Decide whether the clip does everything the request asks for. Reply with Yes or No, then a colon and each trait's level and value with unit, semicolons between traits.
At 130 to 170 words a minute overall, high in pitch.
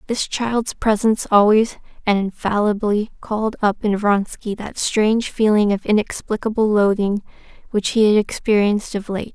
Yes: average, 140 wpm; high, 210 Hz